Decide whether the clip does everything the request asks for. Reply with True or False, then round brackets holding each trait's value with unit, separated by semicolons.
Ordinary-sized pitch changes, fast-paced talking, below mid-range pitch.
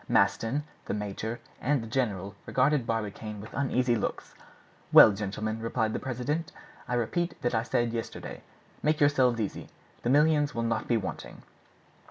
False (3.8 semitones; 155 wpm; 120 Hz)